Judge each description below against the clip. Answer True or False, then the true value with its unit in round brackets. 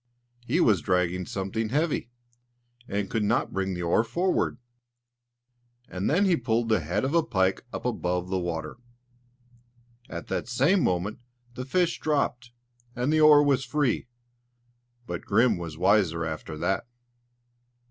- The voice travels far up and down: True (6.9 semitones)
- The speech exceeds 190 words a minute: False (145 wpm)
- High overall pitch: False (110 Hz)